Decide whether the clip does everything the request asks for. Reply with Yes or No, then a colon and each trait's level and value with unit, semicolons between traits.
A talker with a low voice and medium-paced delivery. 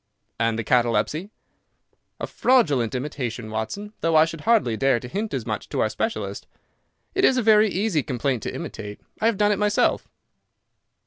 No: medium, 150 Hz; average, 175 wpm